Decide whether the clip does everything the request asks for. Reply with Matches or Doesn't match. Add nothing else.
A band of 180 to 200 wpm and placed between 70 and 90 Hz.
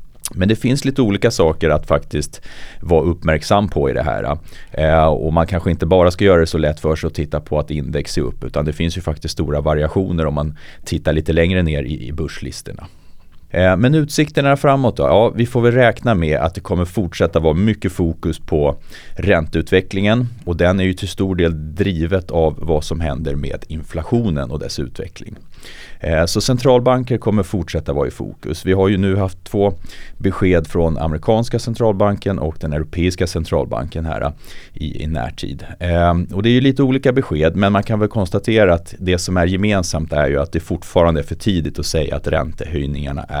Matches